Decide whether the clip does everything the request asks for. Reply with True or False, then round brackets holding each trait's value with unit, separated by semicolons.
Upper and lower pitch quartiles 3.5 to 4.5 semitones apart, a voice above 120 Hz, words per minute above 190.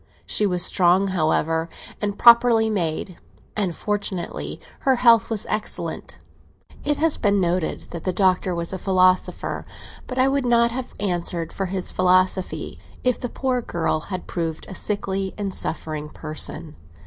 False (4.2 semitones; 190 Hz; 150 wpm)